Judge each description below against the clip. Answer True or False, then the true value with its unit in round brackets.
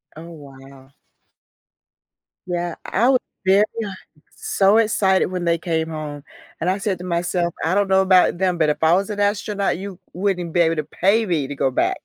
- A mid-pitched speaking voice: True (180 Hz)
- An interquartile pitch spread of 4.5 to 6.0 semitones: False (3.3 semitones)